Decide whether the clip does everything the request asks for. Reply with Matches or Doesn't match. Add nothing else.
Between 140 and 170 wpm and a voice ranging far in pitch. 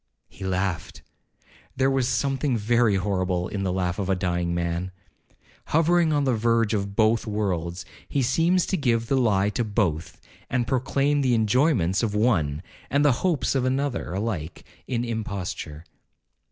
Matches